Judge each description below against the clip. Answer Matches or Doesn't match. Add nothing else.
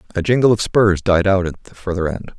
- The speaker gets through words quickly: Matches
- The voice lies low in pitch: Matches